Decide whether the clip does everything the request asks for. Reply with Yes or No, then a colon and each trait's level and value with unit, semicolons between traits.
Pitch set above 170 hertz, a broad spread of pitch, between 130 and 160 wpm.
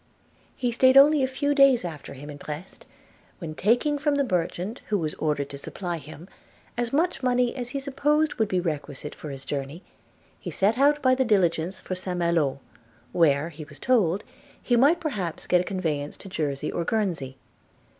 No: medium, 185 Hz; wide, 8.7 semitones; average, 185 wpm